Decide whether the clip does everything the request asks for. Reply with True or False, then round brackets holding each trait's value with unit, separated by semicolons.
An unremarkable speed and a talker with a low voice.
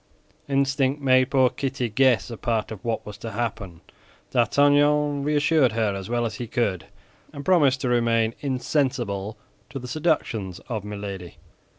True (155 wpm; 120 Hz)